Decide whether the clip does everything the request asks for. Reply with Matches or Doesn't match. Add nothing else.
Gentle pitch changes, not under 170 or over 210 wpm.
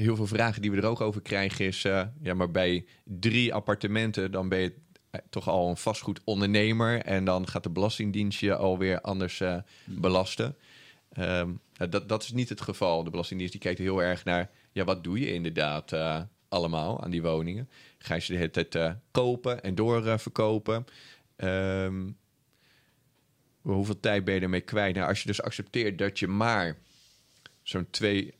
Doesn't match